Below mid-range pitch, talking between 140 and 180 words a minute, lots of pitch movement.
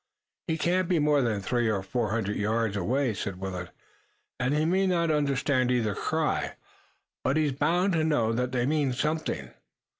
Yes: low, 130 Hz; average, 175 wpm; wide, 5.8 semitones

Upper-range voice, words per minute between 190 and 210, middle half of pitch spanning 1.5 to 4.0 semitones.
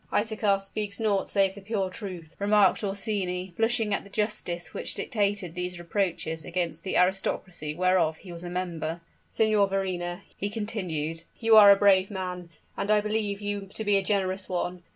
No: high, 195 Hz; average, 175 wpm; narrow, 2.5 semitones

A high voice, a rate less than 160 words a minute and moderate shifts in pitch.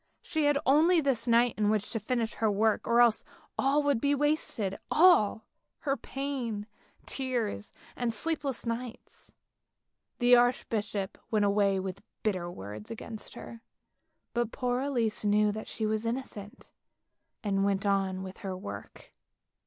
Yes: high, 225 Hz; average, 150 wpm; average, 4.0 semitones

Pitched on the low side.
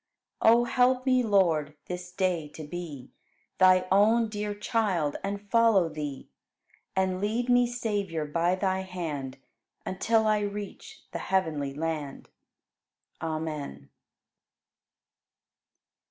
No: medium, 185 Hz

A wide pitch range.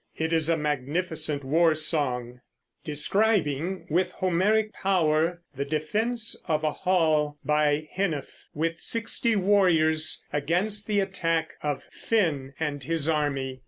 No: average, 3.9 semitones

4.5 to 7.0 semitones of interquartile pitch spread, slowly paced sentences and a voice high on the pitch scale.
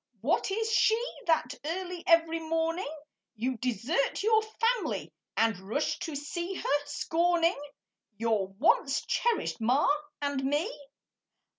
Yes: average, 5.1 semitones; slow, 120 wpm; very high, 320 Hz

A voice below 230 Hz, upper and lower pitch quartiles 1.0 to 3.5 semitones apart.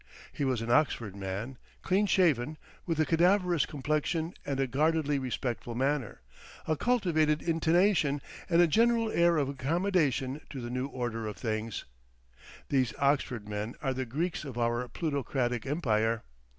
No: medium, 140 Hz; average, 5.2 semitones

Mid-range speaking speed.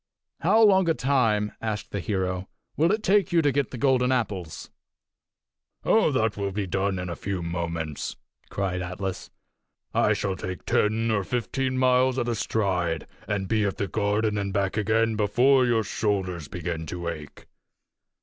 Yes: average, 170 wpm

